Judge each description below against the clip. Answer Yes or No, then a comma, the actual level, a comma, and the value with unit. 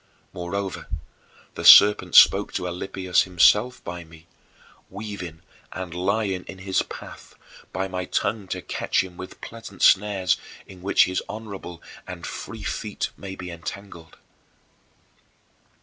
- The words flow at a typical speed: No, slow, 130 wpm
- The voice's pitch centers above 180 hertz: No, very low, 95 Hz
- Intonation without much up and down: Yes, narrow, 2.0 semitones